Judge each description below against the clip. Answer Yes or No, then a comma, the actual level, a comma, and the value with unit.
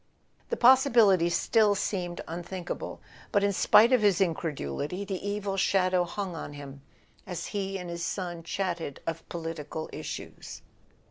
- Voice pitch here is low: No, medium, 185 Hz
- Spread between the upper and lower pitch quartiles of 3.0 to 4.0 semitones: Yes, average, 3.3 semitones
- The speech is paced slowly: No, average, 145 wpm